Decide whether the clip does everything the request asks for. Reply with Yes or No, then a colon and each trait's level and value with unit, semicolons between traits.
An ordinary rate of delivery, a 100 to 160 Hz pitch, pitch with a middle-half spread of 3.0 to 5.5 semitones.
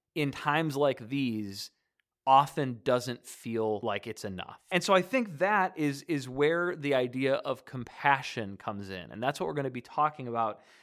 Yes: average, 185 wpm; low, 135 Hz; average, 4.2 semitones